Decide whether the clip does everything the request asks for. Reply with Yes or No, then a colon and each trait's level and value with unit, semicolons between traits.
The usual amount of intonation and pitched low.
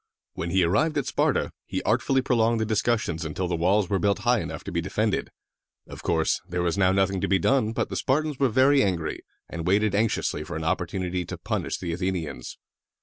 Yes: average, 4.5 semitones; very low, 95 Hz